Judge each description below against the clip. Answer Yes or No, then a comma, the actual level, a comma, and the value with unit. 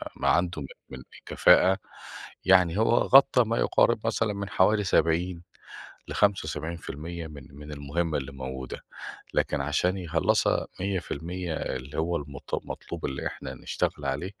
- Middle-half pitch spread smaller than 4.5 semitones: No, average, 4.8 semitones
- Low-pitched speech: Yes, very low, 85 Hz